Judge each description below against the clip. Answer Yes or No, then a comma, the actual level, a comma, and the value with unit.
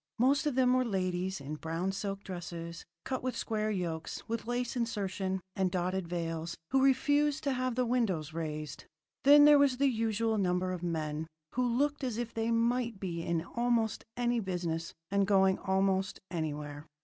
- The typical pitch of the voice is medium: No, high, 195 Hz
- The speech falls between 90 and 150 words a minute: No, average, 175 wpm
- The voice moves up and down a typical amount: No, wide, 6.0 semitones